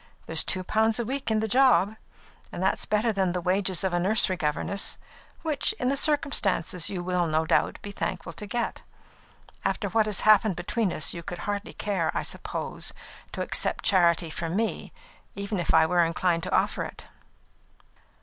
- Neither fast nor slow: Yes, average, 180 wpm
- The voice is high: Yes, high, 195 Hz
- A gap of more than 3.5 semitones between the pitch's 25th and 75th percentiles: Yes, average, 4.0 semitones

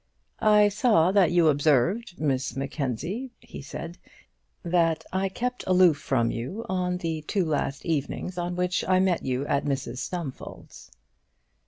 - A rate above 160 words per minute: No, average, 145 wpm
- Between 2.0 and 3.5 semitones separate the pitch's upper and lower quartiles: No, average, 4.8 semitones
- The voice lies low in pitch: No, medium, 170 Hz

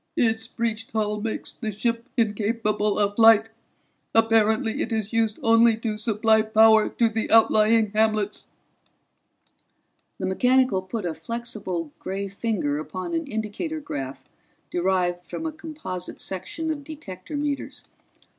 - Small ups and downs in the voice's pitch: Yes, narrow, 2.3 semitones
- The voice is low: No, high, 220 Hz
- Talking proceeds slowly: Yes, slow, 130 wpm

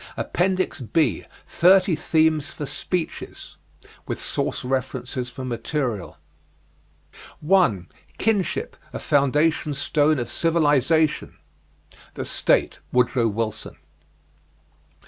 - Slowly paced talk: Yes, slow, 90 wpm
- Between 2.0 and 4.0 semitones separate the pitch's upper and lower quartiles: No, average, 4.6 semitones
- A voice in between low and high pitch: Yes, medium, 145 Hz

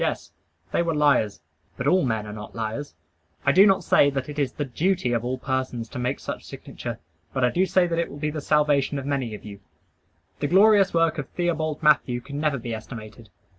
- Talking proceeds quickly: Yes, fast, 220 wpm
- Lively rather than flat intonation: No, average, 4.6 semitones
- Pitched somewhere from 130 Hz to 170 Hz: Yes, medium, 140 Hz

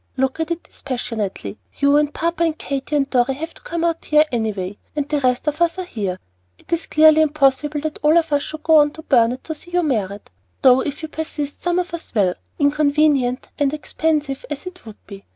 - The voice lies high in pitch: Yes, very high, 295 Hz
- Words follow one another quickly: Yes, fast, 225 wpm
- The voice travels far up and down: No, average, 3.7 semitones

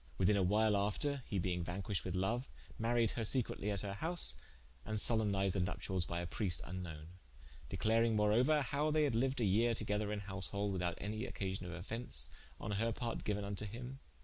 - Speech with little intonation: No, average, 3.4 semitones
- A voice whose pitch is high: No, low, 105 Hz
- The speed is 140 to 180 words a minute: No, average, 190 wpm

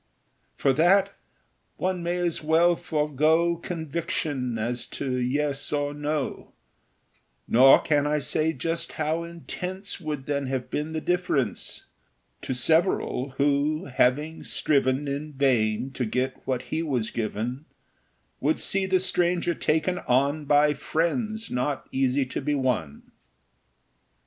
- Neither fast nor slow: No, slow, 130 wpm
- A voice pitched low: No, medium, 150 Hz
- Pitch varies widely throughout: No, average, 3.8 semitones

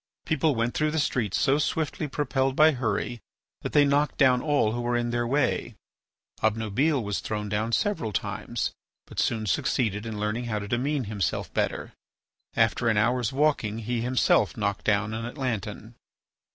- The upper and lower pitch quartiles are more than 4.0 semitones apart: Yes, average, 4.4 semitones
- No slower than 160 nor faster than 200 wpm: Yes, average, 165 wpm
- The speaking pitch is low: Yes, low, 120 Hz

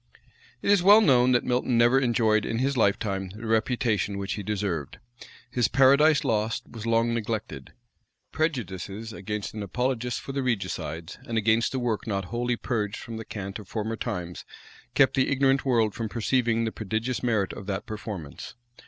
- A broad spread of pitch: No, average, 3.1 semitones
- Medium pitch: No, low, 115 Hz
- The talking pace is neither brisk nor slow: Yes, average, 170 wpm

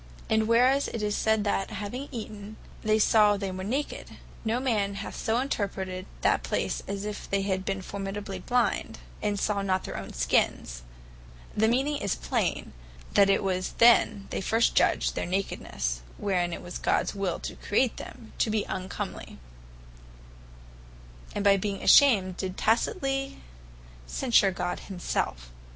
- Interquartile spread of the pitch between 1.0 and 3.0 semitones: Yes, average, 2.7 semitones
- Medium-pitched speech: No, high, 205 Hz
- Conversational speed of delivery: Yes, average, 150 wpm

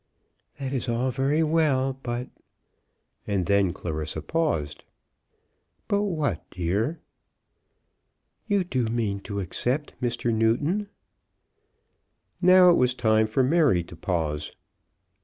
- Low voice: Yes, low, 120 Hz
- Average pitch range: No, wide, 7.2 semitones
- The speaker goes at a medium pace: No, slow, 115 wpm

